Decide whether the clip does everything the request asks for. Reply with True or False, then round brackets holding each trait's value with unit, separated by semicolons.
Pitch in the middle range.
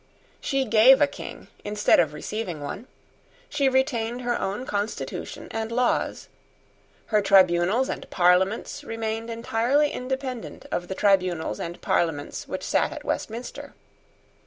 False (225 Hz)